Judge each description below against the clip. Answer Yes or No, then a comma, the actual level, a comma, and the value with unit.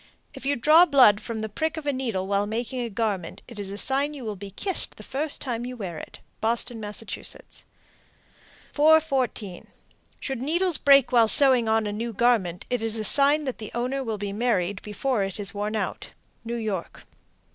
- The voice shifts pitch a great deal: No, average, 4.6 semitones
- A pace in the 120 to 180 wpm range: No, average, 195 wpm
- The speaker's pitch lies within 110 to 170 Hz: No, high, 230 Hz